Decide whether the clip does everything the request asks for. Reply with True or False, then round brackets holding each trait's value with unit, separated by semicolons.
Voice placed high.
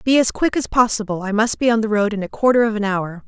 True (220 Hz)